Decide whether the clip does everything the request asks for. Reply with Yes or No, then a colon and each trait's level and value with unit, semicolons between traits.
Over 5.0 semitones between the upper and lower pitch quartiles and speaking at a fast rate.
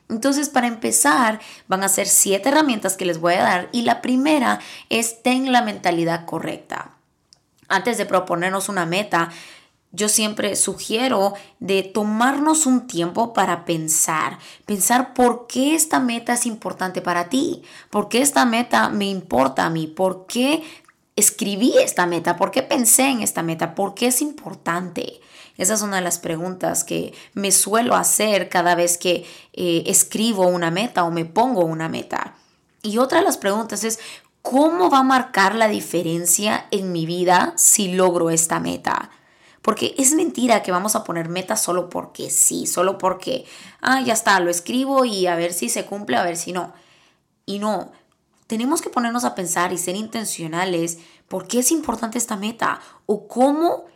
No: wide, 5.4 semitones; average, 170 wpm